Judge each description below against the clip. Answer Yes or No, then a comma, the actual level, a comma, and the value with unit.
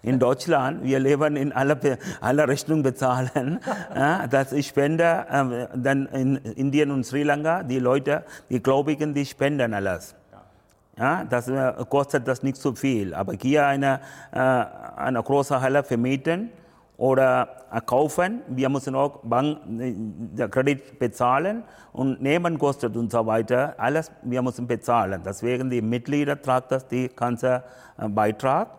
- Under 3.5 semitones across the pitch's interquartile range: Yes, narrow, 2.4 semitones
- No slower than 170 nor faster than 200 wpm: No, average, 150 wpm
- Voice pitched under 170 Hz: Yes, low, 135 Hz